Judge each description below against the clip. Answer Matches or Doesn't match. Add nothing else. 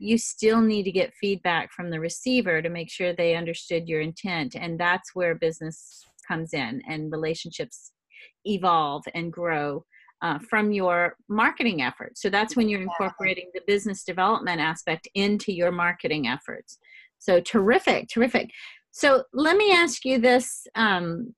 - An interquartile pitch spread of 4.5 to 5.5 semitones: Matches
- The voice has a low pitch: Doesn't match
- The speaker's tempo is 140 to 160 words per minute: Matches